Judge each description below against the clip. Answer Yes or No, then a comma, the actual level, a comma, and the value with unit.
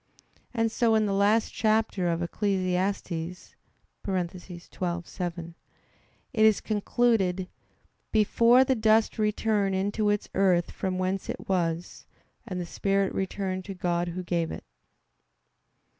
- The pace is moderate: No, slow, 120 wpm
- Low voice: No, high, 195 Hz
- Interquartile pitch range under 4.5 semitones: Yes, average, 3.2 semitones